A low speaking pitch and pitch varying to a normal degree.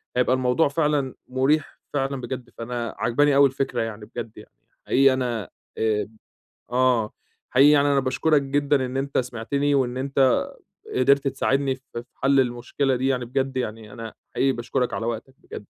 No: low, 130 Hz; narrow, 2.2 semitones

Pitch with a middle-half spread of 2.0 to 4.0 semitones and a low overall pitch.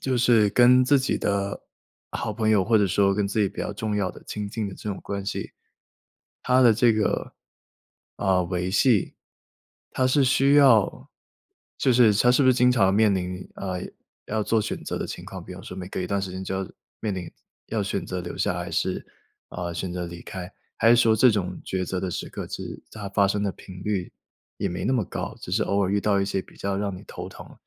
Yes: average, 3.3 semitones; low, 100 Hz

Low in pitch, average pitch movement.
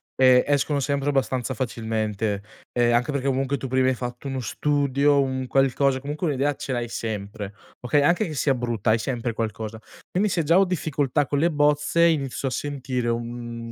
Yes: low, 130 Hz; average, 3.4 semitones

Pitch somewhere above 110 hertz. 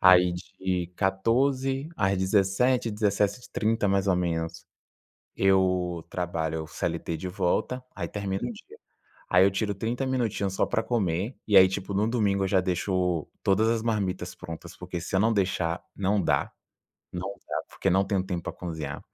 No: very low, 95 Hz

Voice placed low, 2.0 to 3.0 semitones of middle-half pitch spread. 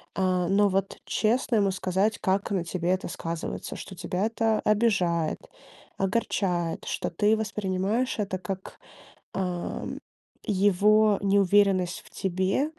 No: high, 195 Hz; narrow, 2.4 semitones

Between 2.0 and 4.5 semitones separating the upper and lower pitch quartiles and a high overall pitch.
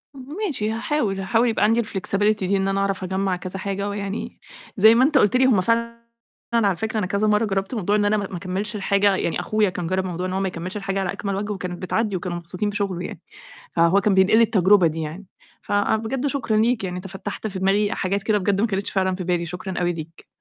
Yes: narrow, 2.4 semitones; high, 195 Hz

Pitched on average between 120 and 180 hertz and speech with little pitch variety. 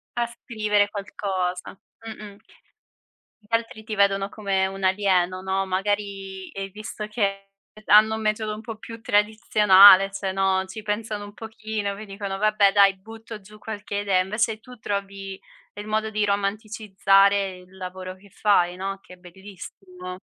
No: high, 200 Hz; narrow, 1.8 semitones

